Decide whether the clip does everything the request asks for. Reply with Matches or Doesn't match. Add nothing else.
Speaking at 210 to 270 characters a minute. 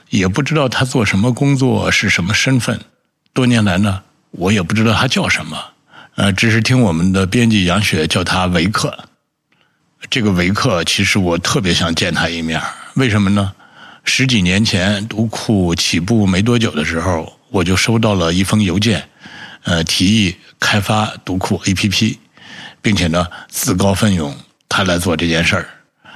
Matches